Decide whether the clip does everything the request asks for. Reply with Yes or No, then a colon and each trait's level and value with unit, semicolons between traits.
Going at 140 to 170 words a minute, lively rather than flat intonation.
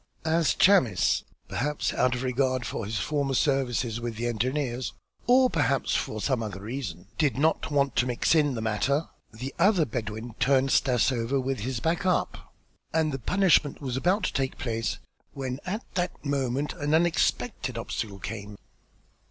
No: average, 165 wpm; average, 4.0 semitones